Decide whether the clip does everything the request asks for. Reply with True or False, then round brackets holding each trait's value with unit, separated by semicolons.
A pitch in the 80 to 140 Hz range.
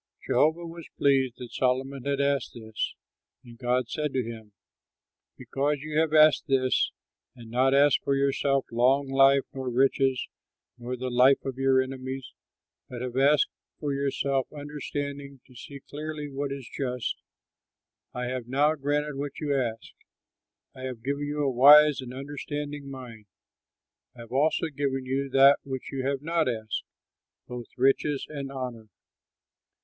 True (135 Hz)